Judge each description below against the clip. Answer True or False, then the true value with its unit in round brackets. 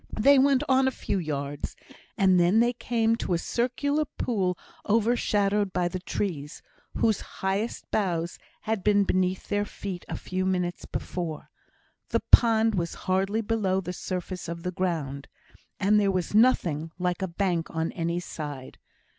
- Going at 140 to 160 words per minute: True (155 wpm)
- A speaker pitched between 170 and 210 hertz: True (190 Hz)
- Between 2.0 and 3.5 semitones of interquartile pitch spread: False (4.0 semitones)